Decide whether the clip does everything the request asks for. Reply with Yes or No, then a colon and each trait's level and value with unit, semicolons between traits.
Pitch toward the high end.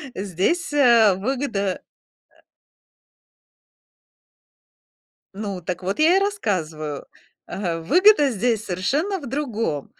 Yes: high, 215 Hz